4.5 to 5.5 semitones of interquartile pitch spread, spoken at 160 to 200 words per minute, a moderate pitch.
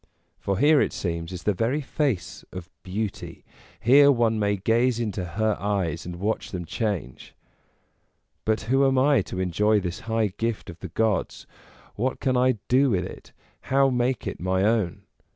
No: average, 5.1 semitones; average, 170 wpm; low, 110 Hz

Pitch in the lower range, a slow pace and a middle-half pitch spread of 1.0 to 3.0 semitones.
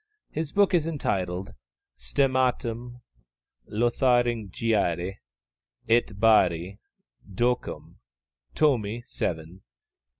No: low, 115 Hz; slow, 65 wpm; average, 4.4 semitones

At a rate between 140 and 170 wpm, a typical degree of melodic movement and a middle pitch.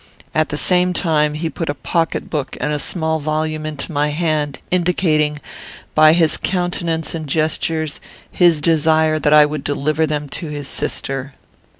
No: average, 160 wpm; narrow, 1.6 semitones; medium, 155 Hz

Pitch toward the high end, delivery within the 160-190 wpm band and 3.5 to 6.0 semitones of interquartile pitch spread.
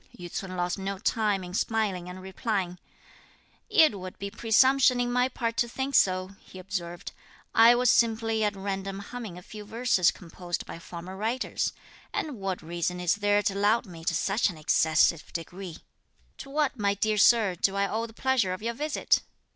Yes: high, 200 Hz; average, 185 wpm; average, 4.0 semitones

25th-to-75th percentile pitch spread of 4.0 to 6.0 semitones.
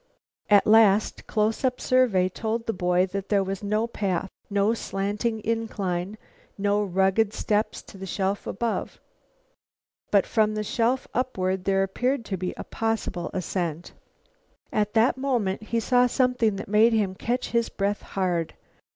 No: average, 2.9 semitones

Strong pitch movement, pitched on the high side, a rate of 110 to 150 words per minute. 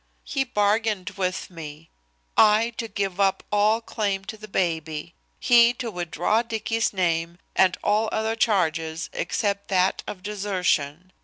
No: average, 3.7 semitones; high, 200 Hz; average, 140 wpm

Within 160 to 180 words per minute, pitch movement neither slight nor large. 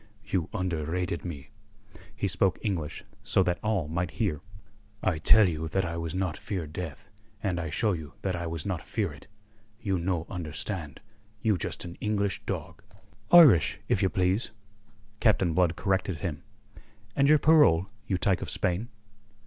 Yes: average, 165 wpm; average, 3.2 semitones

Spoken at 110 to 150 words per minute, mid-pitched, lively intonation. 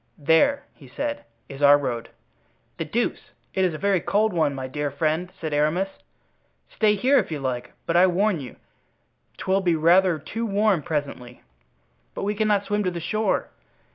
No: average, 175 wpm; medium, 175 Hz; wide, 5.8 semitones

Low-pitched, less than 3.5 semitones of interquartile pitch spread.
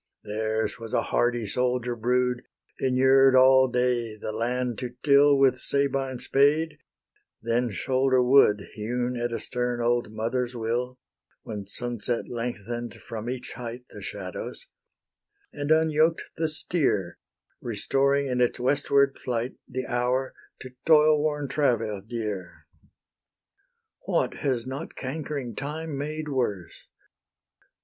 Yes: low, 125 Hz; average, 2.7 semitones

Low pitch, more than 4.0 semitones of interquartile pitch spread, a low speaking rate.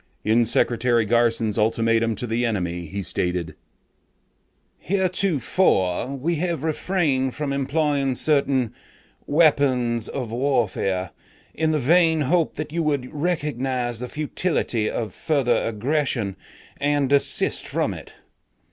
Yes: low, 130 Hz; average, 4.8 semitones; slow, 115 wpm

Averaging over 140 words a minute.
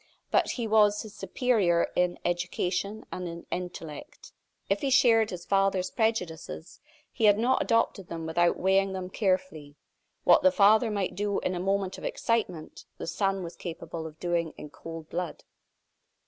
Yes: average, 160 wpm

